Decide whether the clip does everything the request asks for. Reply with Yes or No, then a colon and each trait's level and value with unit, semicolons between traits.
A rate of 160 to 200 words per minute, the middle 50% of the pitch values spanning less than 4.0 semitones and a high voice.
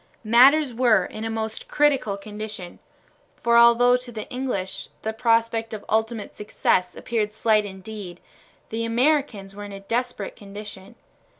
No: average, 140 wpm; narrow, 2.5 semitones; high, 220 Hz